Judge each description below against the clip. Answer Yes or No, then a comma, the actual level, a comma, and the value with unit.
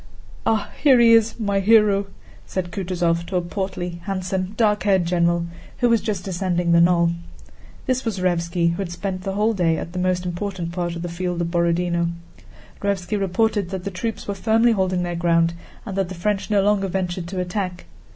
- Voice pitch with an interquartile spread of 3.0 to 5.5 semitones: No, narrow, 2.6 semitones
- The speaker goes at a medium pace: Yes, average, 195 wpm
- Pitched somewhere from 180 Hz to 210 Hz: Yes, medium, 185 Hz